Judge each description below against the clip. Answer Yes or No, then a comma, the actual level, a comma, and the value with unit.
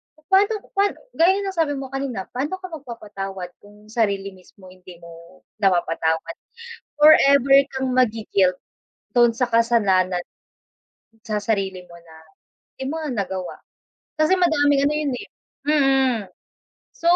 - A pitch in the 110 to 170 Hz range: No, high, 240 Hz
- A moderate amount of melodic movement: No, wide, 7.4 semitones